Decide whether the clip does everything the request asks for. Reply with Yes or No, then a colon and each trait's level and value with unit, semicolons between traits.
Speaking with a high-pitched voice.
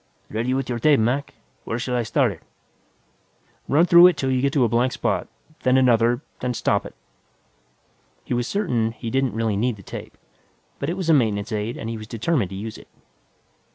No: low, 120 Hz